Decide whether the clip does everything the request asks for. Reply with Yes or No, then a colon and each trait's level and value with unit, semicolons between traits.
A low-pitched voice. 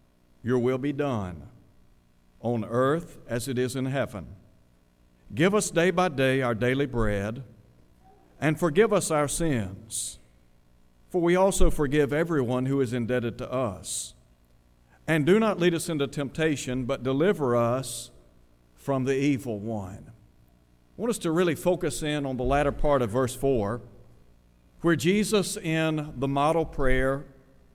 Yes: low, 130 Hz